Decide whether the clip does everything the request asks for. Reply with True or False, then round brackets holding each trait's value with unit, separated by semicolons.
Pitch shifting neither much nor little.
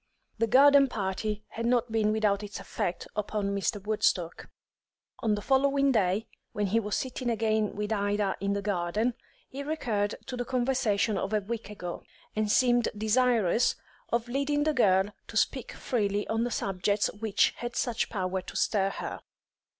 True (3.1 semitones)